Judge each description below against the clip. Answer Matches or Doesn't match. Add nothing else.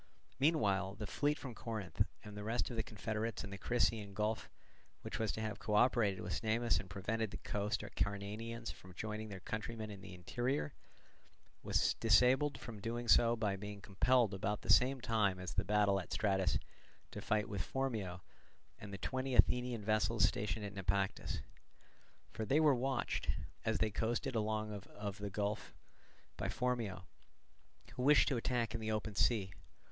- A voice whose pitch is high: Doesn't match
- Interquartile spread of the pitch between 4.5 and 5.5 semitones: Doesn't match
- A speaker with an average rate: Matches